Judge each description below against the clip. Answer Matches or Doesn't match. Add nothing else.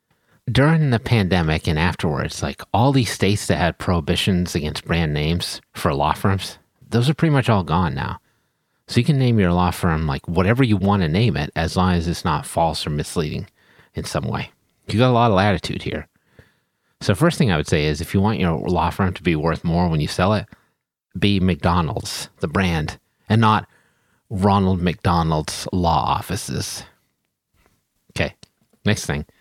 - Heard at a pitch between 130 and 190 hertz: Doesn't match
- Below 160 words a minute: Doesn't match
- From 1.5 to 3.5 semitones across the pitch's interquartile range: Doesn't match